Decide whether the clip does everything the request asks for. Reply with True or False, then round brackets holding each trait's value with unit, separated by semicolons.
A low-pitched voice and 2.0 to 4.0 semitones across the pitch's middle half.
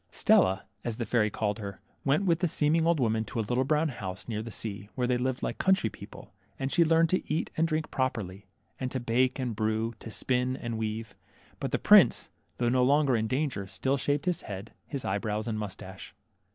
False (120 Hz; 4.6 semitones)